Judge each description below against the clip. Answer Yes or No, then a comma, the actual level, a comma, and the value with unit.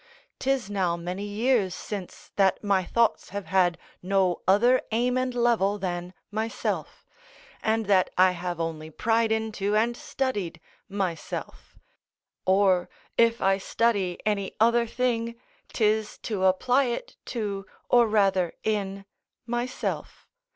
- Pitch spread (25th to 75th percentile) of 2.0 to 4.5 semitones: Yes, average, 3.6 semitones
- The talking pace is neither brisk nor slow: No, slow, 125 wpm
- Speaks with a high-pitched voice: Yes, high, 205 Hz